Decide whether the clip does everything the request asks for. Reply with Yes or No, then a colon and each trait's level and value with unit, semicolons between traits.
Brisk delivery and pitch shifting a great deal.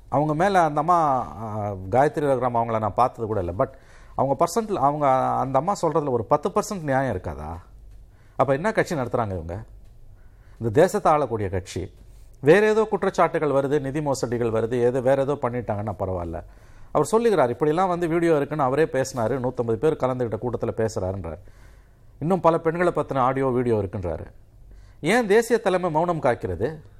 Yes: fast, 155 wpm; wide, 6.5 semitones